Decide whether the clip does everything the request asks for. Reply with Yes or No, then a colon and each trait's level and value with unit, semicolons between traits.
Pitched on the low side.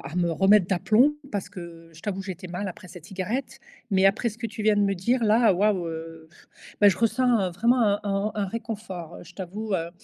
No: high, 195 Hz